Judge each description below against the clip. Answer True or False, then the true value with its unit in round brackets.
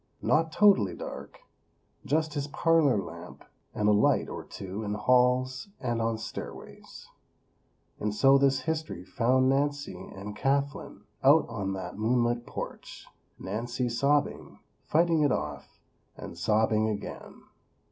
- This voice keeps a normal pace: False (130 wpm)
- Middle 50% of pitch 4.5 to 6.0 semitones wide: True (5.1 semitones)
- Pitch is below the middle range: True (125 Hz)